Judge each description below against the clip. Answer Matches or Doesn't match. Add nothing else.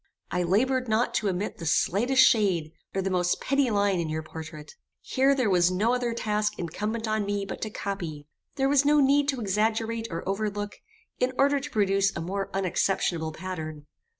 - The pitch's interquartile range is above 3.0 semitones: Matches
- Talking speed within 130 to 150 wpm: Doesn't match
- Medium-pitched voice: Doesn't match